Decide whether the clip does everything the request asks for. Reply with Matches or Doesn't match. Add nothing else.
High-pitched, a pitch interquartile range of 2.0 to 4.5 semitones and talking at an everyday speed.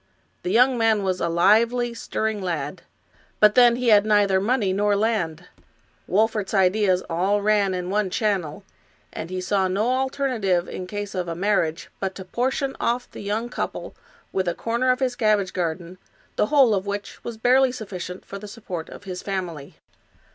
Matches